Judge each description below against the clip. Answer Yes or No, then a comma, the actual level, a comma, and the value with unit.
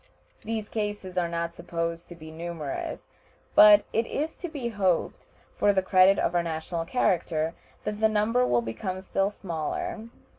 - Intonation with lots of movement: No, average, 3.9 semitones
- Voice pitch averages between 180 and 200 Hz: Yes, medium, 185 Hz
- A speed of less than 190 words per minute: Yes, average, 160 wpm